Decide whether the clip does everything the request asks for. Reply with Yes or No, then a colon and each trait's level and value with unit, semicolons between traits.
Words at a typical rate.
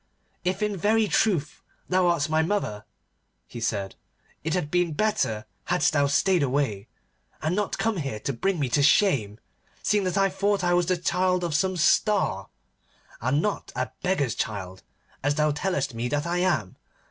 Yes: average, 175 wpm